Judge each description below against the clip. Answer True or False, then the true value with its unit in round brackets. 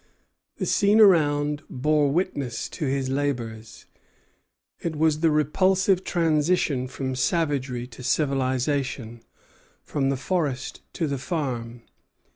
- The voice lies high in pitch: False (145 Hz)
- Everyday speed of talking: False (110 wpm)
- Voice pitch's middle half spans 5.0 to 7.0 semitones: False (3.7 semitones)